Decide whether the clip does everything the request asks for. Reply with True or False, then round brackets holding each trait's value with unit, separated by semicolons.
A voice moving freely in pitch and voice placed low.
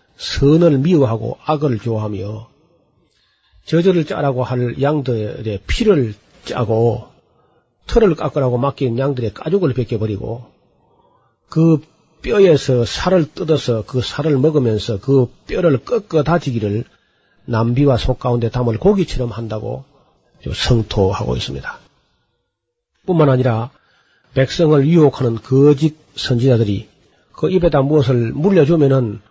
False (4.9 semitones; 130 Hz)